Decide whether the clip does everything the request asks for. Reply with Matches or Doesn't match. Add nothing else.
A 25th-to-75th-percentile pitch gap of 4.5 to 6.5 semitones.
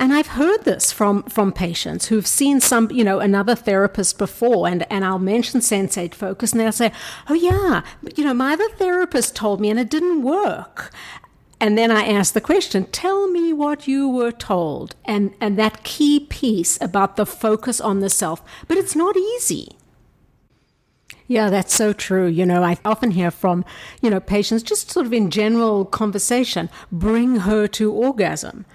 Matches